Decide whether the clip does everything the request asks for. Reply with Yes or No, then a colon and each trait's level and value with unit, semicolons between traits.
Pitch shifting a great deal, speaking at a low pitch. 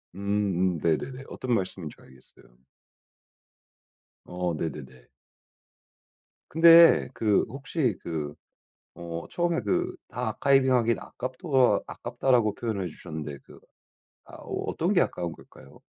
Yes: wide, 7.5 semitones; low, 105 Hz